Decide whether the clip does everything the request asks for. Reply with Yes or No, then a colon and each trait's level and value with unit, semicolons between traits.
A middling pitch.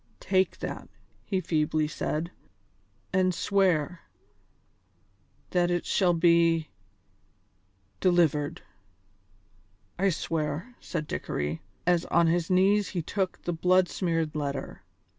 Yes: medium, 170 Hz